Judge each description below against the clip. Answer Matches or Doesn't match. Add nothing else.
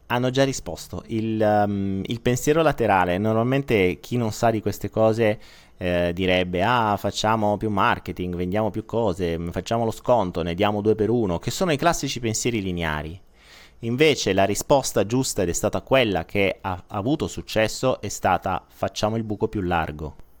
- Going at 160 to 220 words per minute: Matches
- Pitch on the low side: Matches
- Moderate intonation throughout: Matches